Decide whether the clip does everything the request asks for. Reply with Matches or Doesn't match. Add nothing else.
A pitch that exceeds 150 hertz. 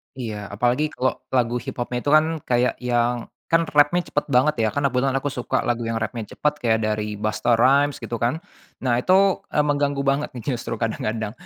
Doesn't match